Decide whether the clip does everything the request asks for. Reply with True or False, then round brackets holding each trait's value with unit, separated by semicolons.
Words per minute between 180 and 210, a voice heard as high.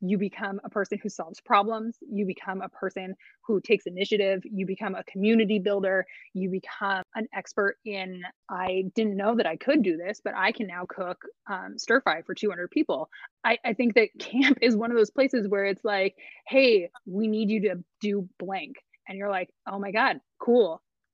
True (200 wpm; 205 Hz)